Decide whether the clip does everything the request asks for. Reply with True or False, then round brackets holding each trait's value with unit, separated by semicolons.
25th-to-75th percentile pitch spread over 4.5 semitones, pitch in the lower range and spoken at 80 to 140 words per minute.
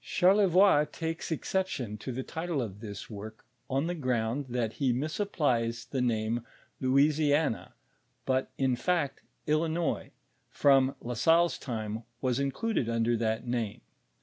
True (5.3 semitones; 130 Hz; 135 wpm)